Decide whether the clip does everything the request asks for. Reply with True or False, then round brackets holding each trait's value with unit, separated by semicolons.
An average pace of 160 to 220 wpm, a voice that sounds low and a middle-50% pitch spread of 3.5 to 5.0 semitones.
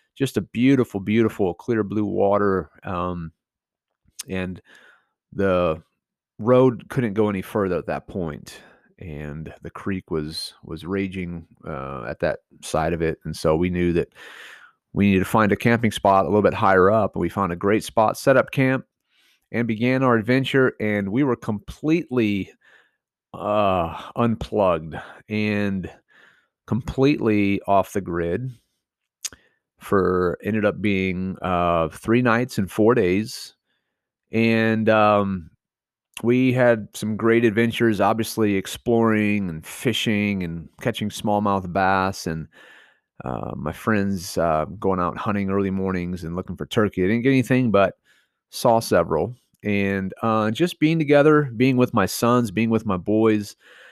False (145 wpm; 105 Hz; 3.9 semitones)